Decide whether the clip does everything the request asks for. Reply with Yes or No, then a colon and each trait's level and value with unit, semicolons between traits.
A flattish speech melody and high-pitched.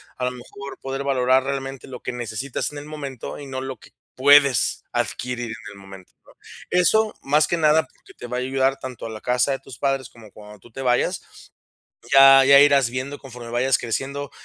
No: narrow, 2.2 semitones; low, 130 Hz